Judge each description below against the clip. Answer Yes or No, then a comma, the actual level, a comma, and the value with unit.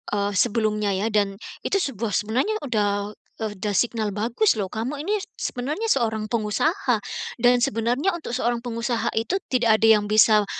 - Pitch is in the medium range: No, high, 225 Hz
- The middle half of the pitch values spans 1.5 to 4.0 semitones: Yes, average, 2.8 semitones